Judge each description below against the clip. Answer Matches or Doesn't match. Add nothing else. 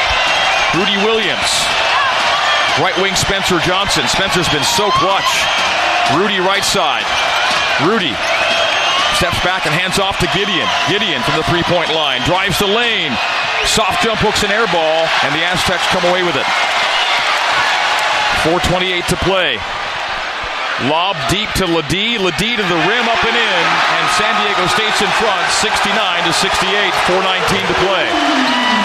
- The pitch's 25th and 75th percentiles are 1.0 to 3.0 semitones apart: Doesn't match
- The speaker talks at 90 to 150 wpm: Matches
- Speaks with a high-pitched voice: Matches